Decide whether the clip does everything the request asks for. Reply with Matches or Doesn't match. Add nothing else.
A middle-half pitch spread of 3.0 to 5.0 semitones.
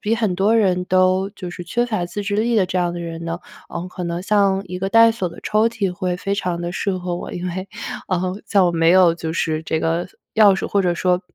Doesn't match